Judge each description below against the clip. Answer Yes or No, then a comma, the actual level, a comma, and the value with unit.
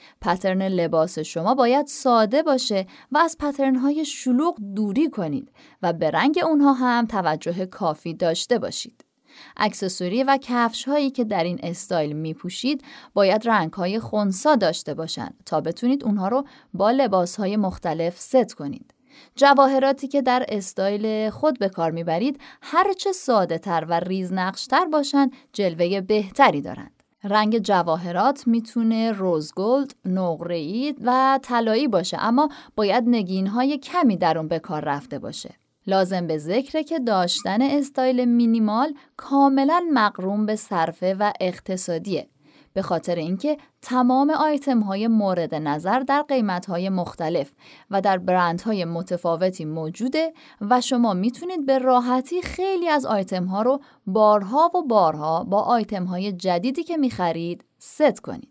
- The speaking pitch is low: No, high, 220 Hz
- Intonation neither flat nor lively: No, wide, 6.7 semitones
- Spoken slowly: No, average, 145 wpm